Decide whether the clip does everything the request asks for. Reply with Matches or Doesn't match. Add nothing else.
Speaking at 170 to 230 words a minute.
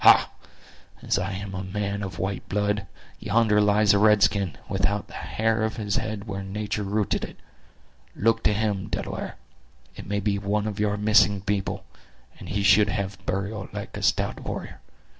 Matches